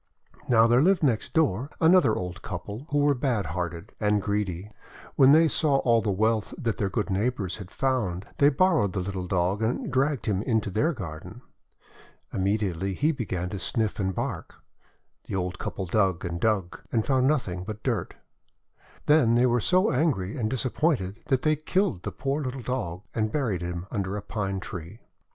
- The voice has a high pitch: No, low, 110 Hz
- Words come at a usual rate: Yes, average, 180 wpm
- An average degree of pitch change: No, wide, 5.8 semitones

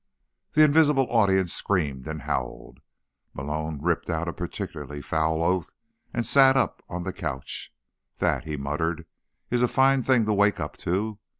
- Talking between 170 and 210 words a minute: No, average, 160 wpm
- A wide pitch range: Yes, wide, 7.2 semitones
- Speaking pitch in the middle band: No, very low, 90 Hz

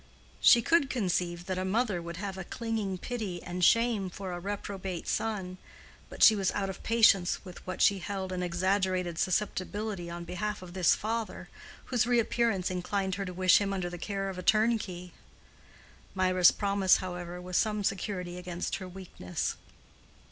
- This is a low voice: No, high, 190 Hz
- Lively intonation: No, narrow, 2.5 semitones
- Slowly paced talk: No, average, 170 wpm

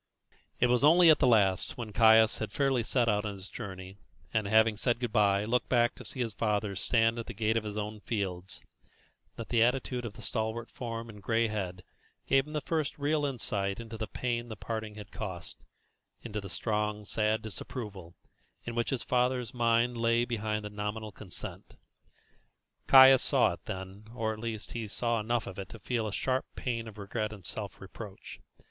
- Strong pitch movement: No, narrow, 2.4 semitones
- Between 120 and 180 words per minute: No, average, 195 wpm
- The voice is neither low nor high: No, low, 110 Hz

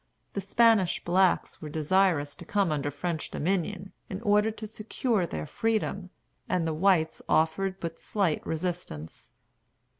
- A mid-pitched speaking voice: Yes, medium, 180 Hz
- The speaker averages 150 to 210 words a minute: No, average, 140 wpm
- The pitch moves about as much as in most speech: Yes, average, 3.9 semitones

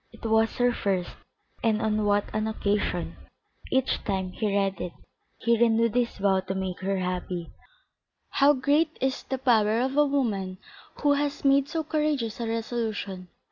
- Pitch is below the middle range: No, high, 225 Hz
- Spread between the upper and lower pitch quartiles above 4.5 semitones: Yes, average, 5.1 semitones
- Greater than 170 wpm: No, average, 165 wpm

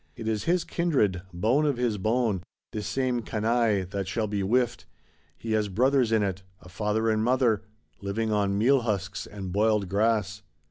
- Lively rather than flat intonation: No, average, 3.1 semitones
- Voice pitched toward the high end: No, low, 110 Hz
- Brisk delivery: No, average, 170 wpm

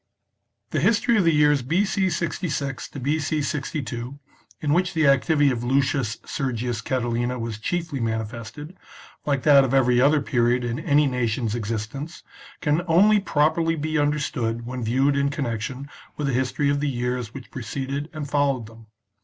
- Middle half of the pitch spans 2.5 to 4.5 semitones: Yes, average, 3.6 semitones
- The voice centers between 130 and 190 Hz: Yes, medium, 140 Hz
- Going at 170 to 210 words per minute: No, average, 160 wpm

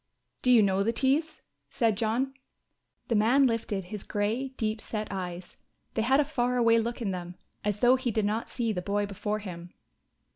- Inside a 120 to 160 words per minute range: No, average, 190 wpm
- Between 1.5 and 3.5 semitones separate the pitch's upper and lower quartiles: Yes, average, 3.2 semitones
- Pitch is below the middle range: No, high, 220 Hz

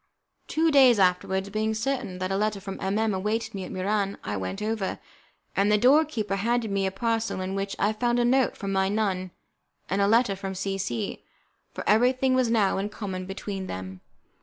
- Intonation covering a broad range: No, average, 2.9 semitones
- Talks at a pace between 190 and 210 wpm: Yes, fast, 205 wpm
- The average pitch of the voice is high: Yes, high, 200 Hz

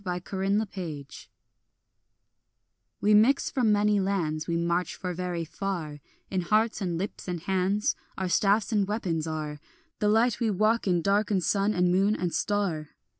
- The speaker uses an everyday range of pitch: Yes, average, 3.4 semitones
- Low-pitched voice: No, high, 190 Hz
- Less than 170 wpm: Yes, average, 160 wpm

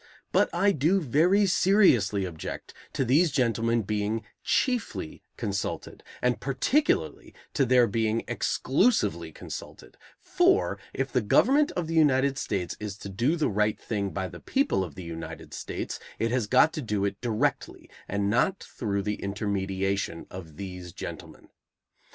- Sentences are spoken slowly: No, average, 150 wpm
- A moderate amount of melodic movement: No, wide, 7.8 semitones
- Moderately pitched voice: No, low, 115 Hz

